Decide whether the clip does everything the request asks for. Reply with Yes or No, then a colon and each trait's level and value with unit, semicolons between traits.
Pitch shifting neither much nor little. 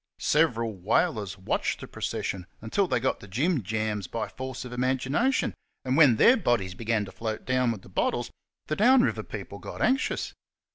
No: wide, 5.9 semitones